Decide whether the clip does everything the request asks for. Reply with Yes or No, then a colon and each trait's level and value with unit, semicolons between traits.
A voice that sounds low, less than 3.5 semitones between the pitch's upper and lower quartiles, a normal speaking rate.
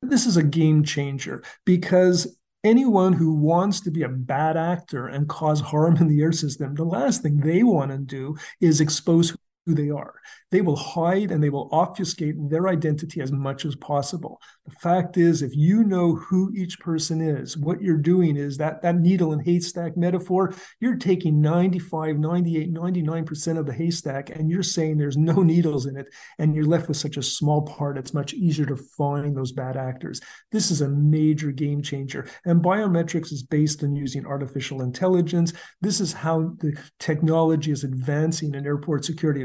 No: medium, 160 Hz; average, 2.9 semitones; average, 185 wpm